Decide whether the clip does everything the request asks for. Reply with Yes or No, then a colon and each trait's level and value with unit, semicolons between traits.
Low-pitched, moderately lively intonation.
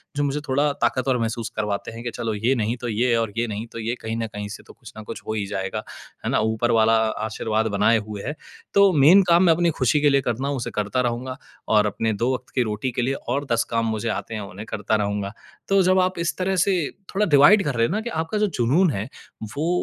Yes: low, 120 Hz; average, 4.9 semitones